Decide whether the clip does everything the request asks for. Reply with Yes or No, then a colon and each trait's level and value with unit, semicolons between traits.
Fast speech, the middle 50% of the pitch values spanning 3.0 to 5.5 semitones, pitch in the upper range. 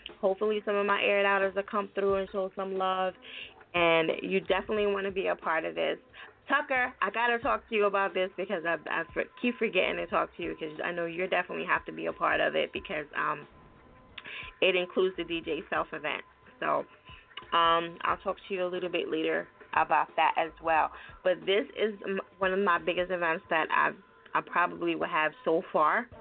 No: fast, 210 wpm; narrow, 2.4 semitones; high, 195 Hz